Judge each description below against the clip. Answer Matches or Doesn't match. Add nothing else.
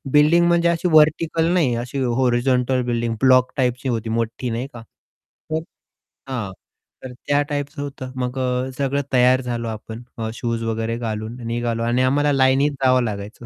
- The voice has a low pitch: Matches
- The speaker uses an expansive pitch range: Doesn't match